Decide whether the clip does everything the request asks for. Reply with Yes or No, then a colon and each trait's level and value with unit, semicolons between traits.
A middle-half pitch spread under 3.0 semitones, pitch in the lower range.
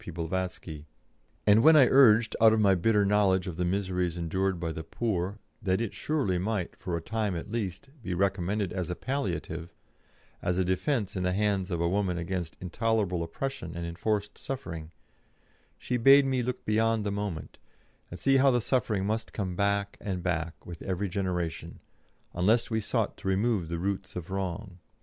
No: average, 3.7 semitones; very low, 95 Hz